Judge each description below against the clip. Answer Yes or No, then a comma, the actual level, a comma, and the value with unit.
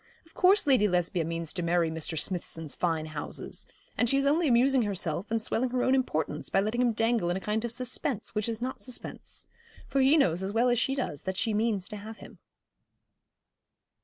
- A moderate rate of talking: No, fast, 210 wpm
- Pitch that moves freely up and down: Yes, wide, 6.1 semitones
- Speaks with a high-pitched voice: Yes, high, 220 Hz